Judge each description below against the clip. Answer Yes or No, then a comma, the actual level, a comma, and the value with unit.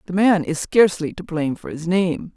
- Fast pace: Yes, fast, 230 wpm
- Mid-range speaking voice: Yes, medium, 175 Hz